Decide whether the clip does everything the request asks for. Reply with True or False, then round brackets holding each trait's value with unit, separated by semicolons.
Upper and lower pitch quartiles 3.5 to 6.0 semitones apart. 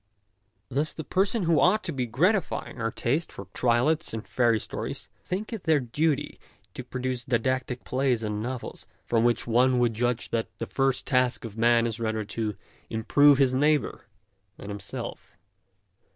True (4.0 semitones)